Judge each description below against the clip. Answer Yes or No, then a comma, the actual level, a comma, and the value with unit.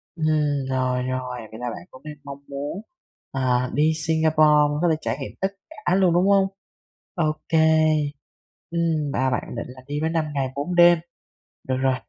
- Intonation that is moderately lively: Yes, average, 4.1 semitones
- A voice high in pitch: No, medium, 150 Hz